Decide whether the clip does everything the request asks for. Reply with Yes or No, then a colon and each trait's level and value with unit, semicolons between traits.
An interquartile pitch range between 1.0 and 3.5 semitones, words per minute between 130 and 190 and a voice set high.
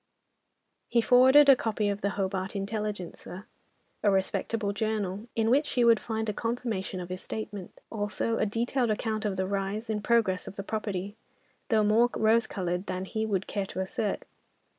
Yes: average, 2.7 semitones; average, 175 wpm; high, 210 Hz